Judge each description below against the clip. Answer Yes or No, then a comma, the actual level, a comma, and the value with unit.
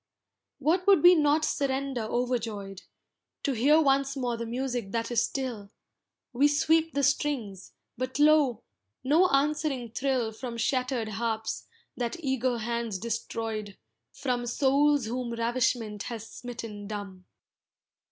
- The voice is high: Yes, high, 245 Hz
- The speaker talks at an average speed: No, slow, 125 wpm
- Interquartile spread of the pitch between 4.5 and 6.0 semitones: No, average, 3.6 semitones